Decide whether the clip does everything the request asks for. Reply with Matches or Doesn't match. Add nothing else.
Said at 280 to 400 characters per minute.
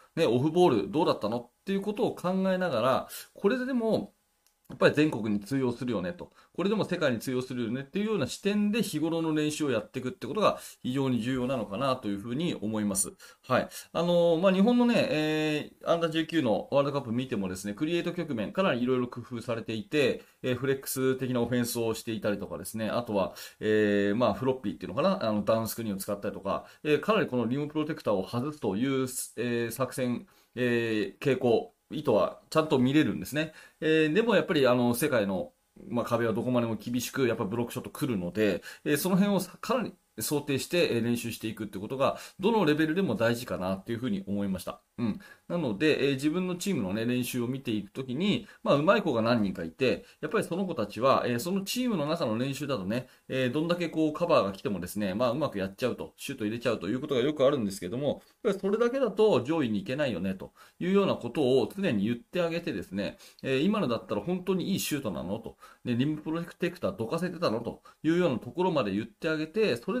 Doesn't match